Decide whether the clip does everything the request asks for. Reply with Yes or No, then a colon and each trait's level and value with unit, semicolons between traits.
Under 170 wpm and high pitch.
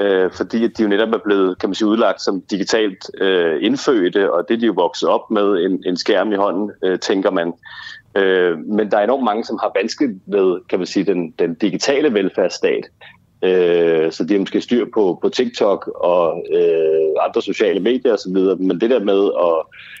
No: average, 200 wpm; very high, 375 Hz